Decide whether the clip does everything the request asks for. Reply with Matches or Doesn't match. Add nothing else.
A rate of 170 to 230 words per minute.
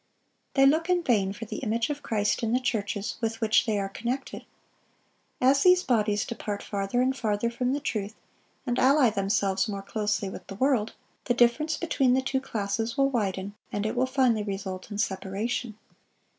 Matches